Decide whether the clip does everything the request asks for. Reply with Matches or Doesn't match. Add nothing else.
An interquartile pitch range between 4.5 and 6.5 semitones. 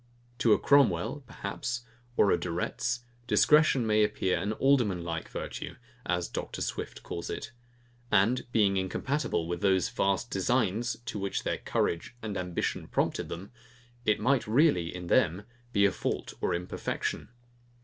Matches